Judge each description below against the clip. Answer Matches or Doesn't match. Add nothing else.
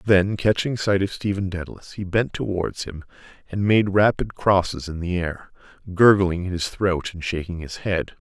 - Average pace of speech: Matches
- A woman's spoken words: Doesn't match